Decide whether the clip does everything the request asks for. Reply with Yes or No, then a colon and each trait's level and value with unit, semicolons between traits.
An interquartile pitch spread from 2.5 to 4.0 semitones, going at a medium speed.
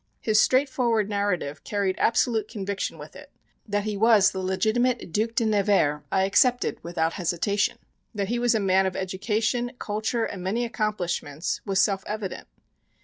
Yes: average, 3.0 semitones; average, 155 wpm